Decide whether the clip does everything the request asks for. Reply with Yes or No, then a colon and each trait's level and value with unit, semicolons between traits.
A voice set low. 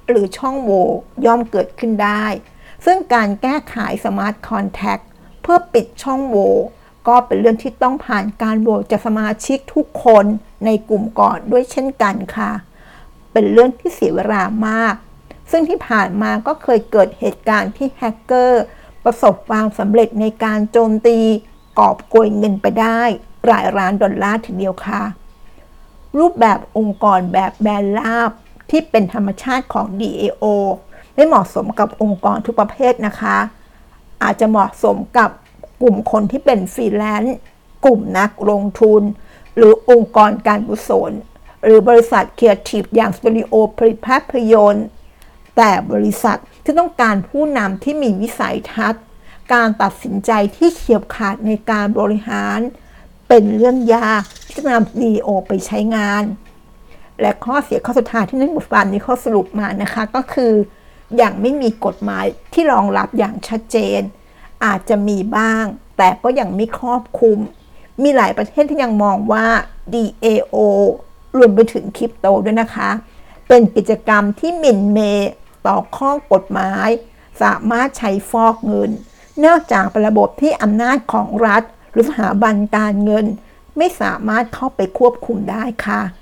No: high, 220 Hz